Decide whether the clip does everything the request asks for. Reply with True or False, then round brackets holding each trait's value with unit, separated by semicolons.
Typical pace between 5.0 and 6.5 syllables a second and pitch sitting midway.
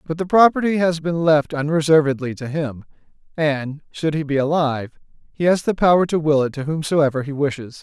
True (5.4 syllables/s; 155 Hz)